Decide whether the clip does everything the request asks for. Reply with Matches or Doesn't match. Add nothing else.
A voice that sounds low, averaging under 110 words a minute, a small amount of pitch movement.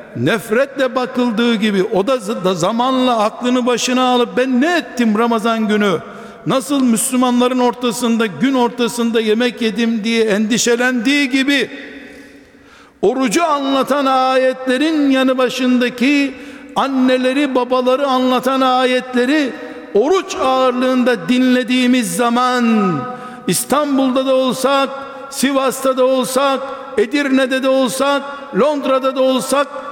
Doesn't match